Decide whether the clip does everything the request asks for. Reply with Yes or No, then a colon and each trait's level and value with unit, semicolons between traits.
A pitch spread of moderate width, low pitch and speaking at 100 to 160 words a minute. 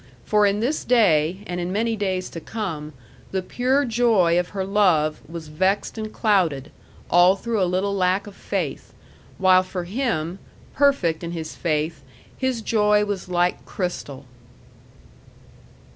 No: average, 3.6 semitones; medium, 185 Hz; average, 145 wpm